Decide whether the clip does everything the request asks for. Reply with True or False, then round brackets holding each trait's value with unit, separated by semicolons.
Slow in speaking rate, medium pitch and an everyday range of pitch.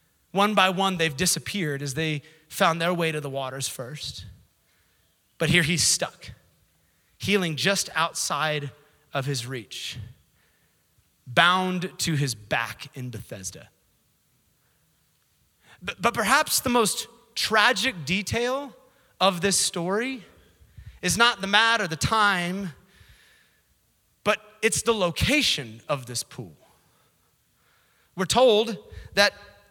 False (115 wpm; 165 Hz; 7.7 semitones)